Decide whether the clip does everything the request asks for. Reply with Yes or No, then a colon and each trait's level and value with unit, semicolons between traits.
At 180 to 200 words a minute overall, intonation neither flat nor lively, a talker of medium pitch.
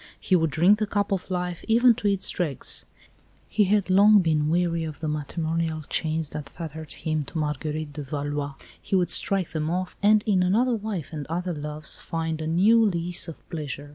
Yes: average, 195 wpm; average, 3.9 semitones; medium, 165 Hz